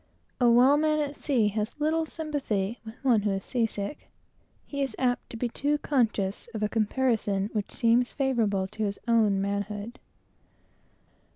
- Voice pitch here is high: Yes, high, 230 Hz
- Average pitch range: Yes, average, 4.8 semitones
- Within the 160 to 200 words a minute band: No, average, 150 wpm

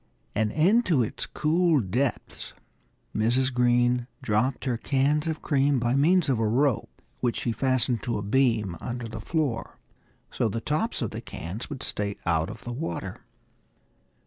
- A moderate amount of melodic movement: Yes, average, 4.2 semitones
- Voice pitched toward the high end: No, low, 125 Hz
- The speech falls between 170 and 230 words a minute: No, average, 160 wpm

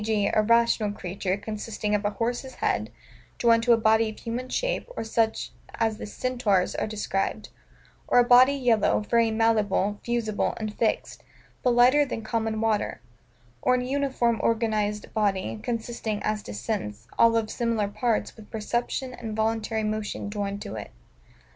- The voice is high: Yes, high, 220 Hz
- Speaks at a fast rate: No, average, 160 wpm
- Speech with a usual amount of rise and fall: No, narrow, 2.1 semitones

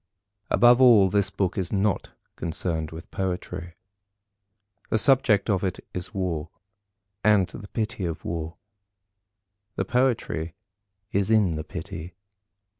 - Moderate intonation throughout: Yes, average, 4.0 semitones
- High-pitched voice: No, very low, 95 Hz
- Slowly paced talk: Yes, slow, 120 wpm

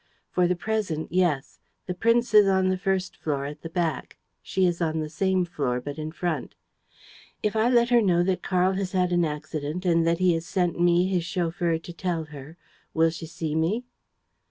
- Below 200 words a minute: No, fast, 205 wpm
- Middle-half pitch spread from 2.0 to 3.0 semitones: Yes, average, 2.7 semitones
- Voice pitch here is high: No, medium, 175 Hz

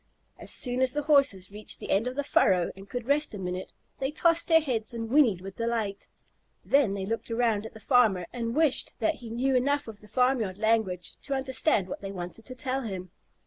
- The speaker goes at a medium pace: No, fast, 220 wpm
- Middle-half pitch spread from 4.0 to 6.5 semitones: Yes, average, 5.0 semitones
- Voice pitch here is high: Yes, high, 230 Hz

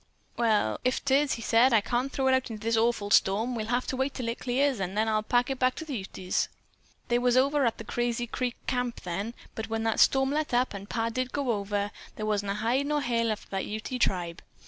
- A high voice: Yes, high, 235 Hz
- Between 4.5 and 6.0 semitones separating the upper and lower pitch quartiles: No, average, 3.1 semitones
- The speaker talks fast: Yes, fast, 255 wpm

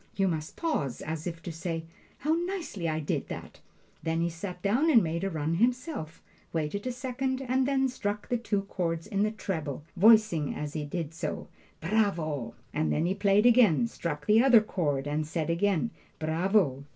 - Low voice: No, medium, 180 Hz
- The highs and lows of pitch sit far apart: Yes, wide, 6.2 semitones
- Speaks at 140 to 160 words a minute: No, average, 185 wpm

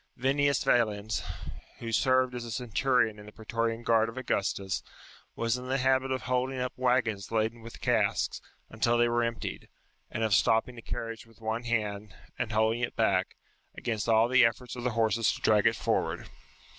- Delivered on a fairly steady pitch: Yes, narrow, 2.1 semitones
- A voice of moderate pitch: No, low, 115 Hz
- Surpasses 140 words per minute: Yes, average, 180 wpm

